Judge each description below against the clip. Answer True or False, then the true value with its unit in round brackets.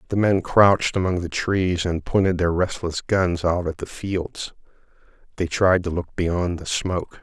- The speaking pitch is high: False (90 Hz)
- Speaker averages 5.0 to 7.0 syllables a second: False (4.4 syllables/s)